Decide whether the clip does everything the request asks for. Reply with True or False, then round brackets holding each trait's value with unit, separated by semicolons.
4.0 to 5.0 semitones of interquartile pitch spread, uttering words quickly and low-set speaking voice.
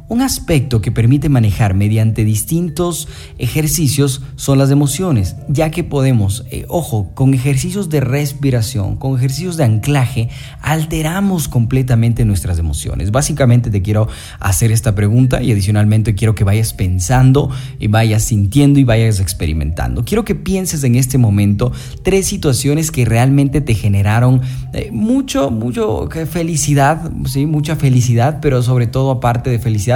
False (4.7 semitones; 140 wpm; 130 Hz)